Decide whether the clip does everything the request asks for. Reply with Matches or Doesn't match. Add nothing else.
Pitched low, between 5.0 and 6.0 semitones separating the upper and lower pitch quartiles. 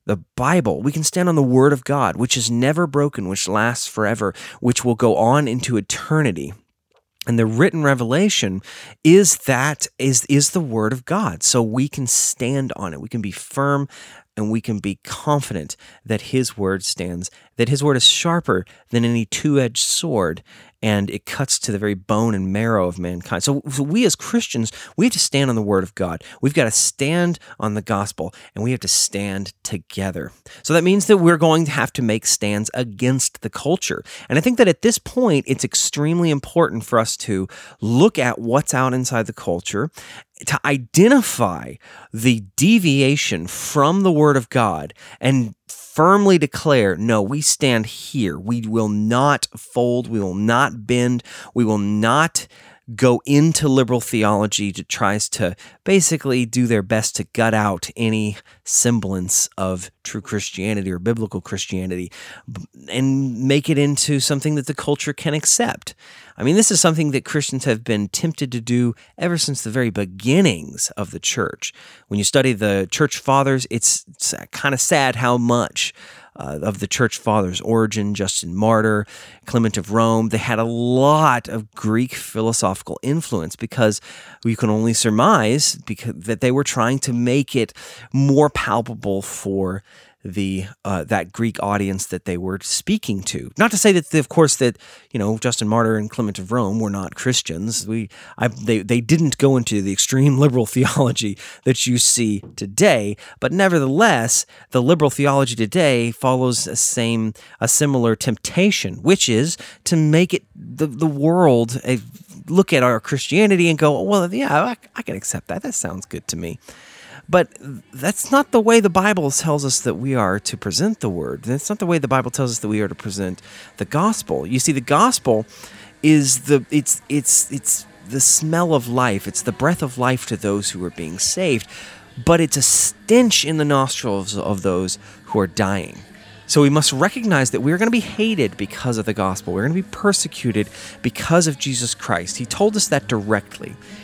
Matches